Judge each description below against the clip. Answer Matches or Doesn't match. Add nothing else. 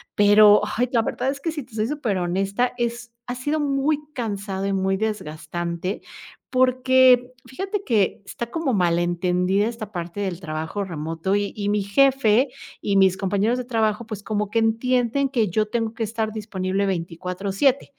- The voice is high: Matches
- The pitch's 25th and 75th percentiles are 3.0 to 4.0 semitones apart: Doesn't match